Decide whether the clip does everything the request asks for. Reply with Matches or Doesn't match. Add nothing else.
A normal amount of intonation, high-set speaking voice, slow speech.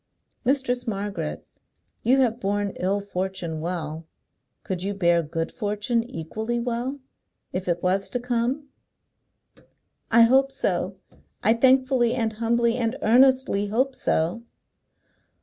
Matches